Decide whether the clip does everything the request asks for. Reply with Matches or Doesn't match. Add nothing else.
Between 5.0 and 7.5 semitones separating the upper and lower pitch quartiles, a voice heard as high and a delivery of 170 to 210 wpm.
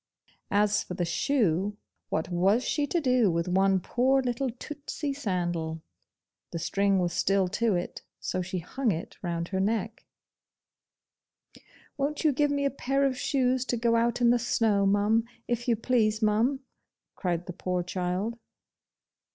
Doesn't match